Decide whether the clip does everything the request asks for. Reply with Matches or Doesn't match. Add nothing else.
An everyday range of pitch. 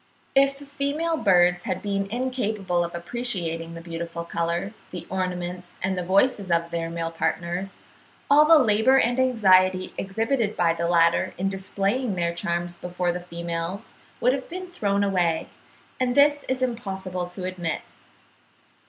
Doesn't match